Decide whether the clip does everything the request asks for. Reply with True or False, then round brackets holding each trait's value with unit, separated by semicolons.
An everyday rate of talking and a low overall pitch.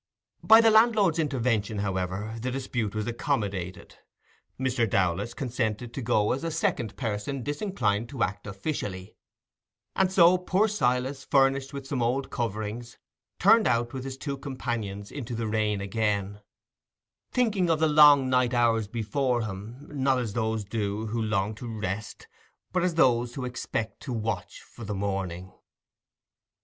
True (150 wpm; 120 Hz)